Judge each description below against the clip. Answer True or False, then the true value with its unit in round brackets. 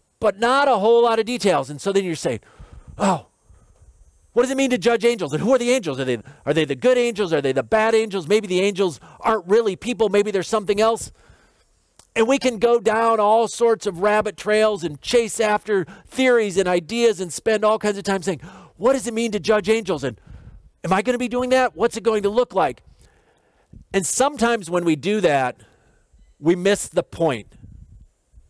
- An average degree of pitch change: True (4.6 semitones)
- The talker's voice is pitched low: False (210 Hz)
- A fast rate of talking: True (215 wpm)